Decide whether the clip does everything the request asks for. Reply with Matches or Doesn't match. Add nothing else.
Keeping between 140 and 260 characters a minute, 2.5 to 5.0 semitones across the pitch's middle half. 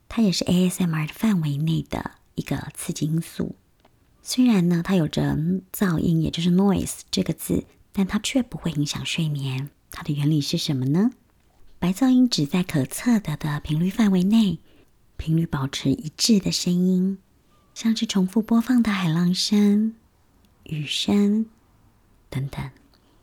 Doesn't match